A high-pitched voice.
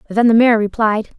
Yes: high, 220 Hz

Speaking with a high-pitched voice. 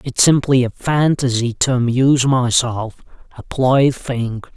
No: low, 130 Hz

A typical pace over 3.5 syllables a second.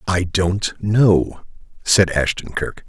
No: 3.0 syllables/s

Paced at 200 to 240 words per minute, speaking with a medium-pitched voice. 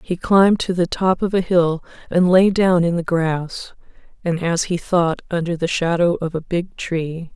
Yes: fast, 205 wpm; medium, 175 Hz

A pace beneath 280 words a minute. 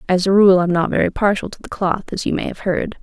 No: fast, 300 wpm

